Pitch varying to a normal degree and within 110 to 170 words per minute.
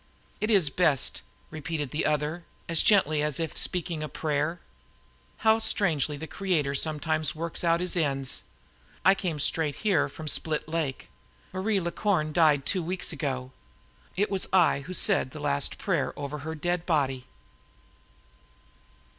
Yes: average, 3.4 semitones; average, 150 wpm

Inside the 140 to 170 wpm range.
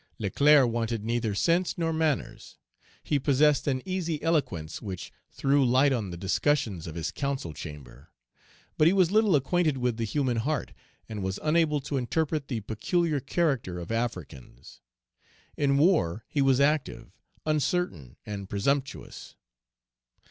Yes: average, 150 wpm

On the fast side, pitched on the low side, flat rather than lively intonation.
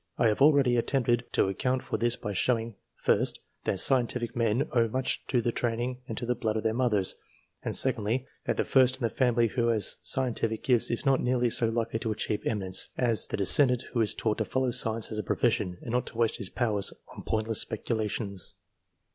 Yes: fast, 215 wpm; low, 115 Hz; narrow, 2.2 semitones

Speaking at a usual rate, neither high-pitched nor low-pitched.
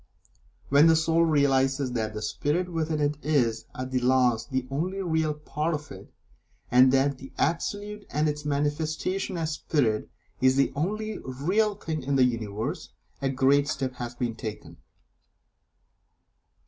Yes: average, 150 wpm; medium, 145 Hz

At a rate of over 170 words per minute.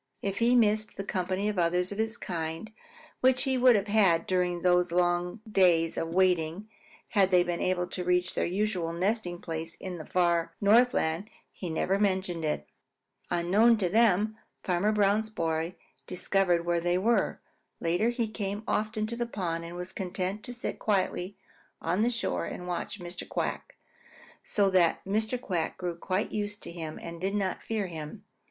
Yes: average, 180 wpm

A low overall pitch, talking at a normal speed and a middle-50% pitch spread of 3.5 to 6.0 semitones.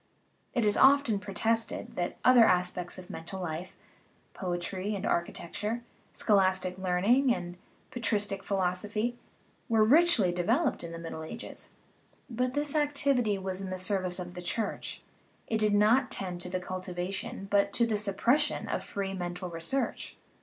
No: high, 195 Hz; average, 150 wpm; average, 4.2 semitones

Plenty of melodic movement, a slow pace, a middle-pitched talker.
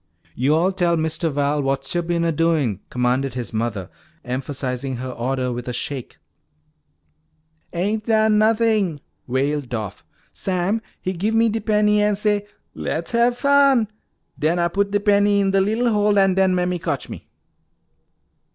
No: wide, 7.5 semitones; average, 155 wpm; medium, 175 Hz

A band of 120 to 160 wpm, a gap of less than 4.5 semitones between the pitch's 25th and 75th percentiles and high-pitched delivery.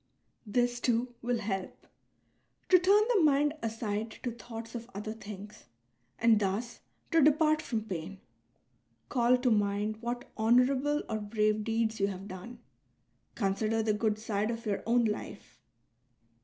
Yes: average, 145 wpm; average, 2.7 semitones; high, 225 Hz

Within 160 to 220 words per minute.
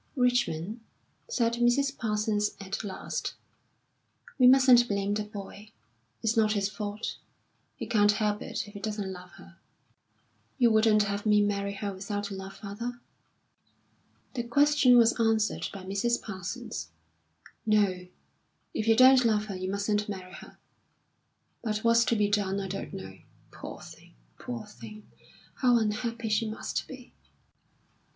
No: average, 145 wpm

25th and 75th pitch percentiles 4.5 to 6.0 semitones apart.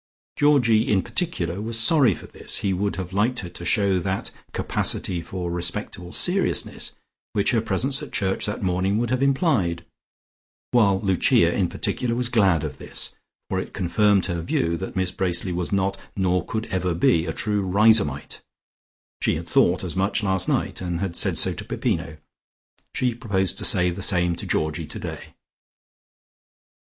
No: average, 3.8 semitones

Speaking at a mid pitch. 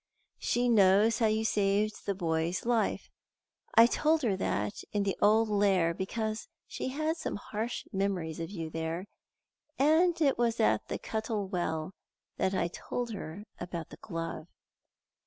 No: high, 205 Hz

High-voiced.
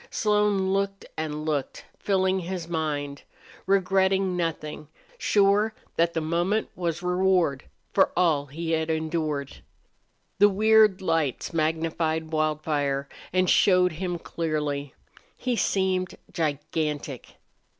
No: medium, 165 Hz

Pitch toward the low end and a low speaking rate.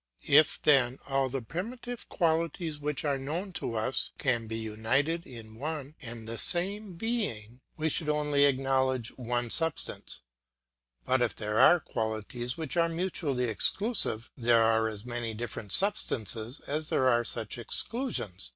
No: low, 130 Hz; average, 150 wpm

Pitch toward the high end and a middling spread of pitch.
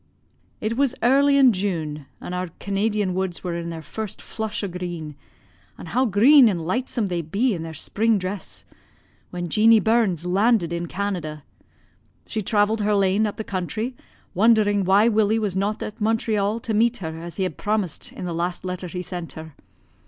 Yes: high, 200 Hz; average, 3.8 semitones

